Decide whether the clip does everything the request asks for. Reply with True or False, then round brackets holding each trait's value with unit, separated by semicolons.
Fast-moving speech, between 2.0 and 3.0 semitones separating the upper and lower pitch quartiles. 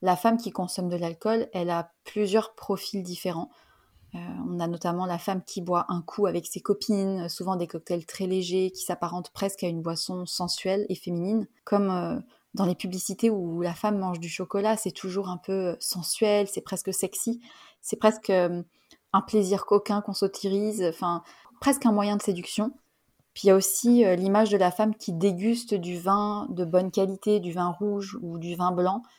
False (195 wpm; 2.6 semitones)